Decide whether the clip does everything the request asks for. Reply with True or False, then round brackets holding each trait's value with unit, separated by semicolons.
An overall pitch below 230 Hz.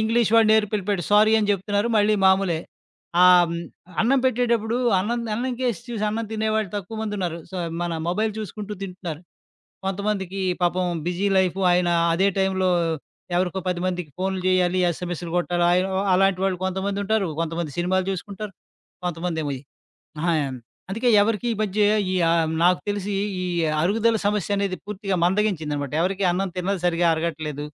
True (190 Hz)